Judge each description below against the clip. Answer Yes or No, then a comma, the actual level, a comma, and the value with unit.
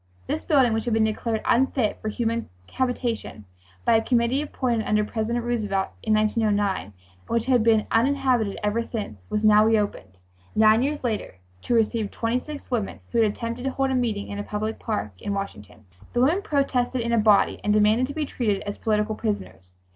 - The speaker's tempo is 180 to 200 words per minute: Yes, average, 190 wpm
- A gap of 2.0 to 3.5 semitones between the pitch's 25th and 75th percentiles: Yes, average, 2.7 semitones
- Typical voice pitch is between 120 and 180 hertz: No, high, 225 Hz